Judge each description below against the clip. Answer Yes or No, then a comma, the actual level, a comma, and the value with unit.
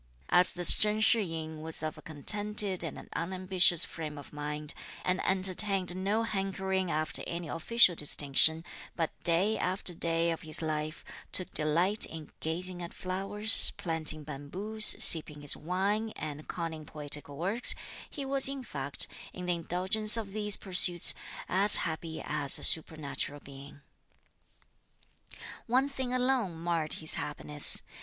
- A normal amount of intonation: Yes, average, 4.1 semitones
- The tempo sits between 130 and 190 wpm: Yes, average, 140 wpm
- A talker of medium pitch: Yes, medium, 175 Hz